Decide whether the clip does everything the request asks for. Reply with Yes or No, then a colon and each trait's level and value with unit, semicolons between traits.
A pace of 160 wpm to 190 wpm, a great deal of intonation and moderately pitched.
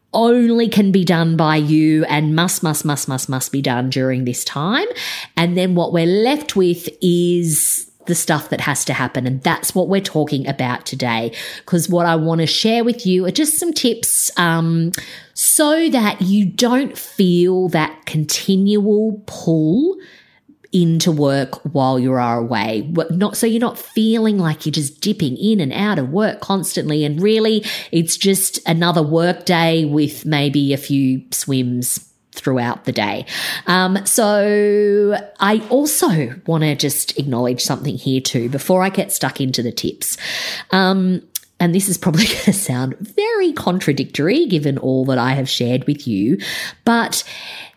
Yes: average, 165 wpm; wide, 6.2 semitones; medium, 170 Hz